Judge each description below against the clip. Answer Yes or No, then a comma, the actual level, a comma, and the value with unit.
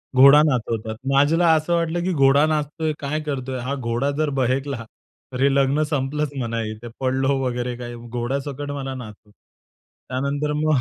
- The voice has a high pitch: No, low, 135 Hz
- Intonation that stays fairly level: No, average, 3.0 semitones